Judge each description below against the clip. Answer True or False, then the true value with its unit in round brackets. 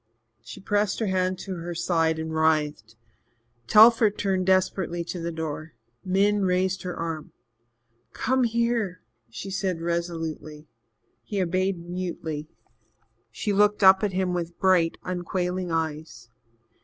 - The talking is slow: True (130 wpm)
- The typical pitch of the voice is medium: True (180 Hz)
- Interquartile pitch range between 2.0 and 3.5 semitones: True (2.8 semitones)